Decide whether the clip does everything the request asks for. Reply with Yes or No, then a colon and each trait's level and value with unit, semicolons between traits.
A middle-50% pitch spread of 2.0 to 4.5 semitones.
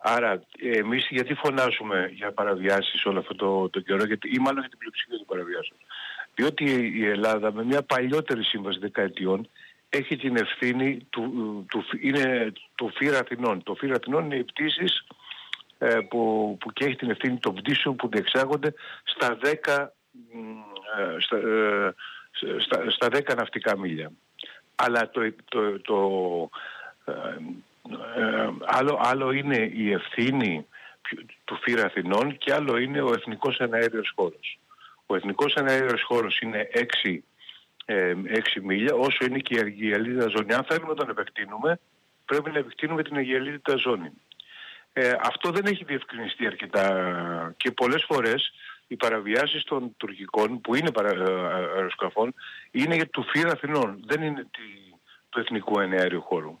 No: average, 5.3 semitones